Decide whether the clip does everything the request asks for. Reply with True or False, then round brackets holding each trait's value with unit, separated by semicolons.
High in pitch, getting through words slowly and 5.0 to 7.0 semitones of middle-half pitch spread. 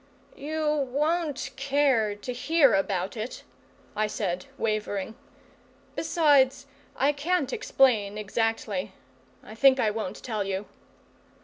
True (245 Hz; 110 wpm; 5.3 semitones)